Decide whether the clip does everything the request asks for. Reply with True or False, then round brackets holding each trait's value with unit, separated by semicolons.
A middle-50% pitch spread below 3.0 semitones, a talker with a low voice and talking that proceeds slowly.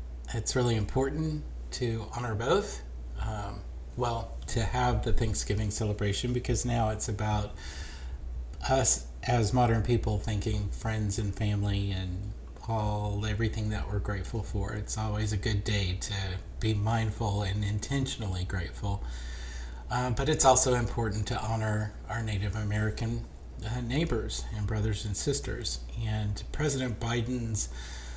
True (2.6 semitones; 105 Hz; 130 wpm)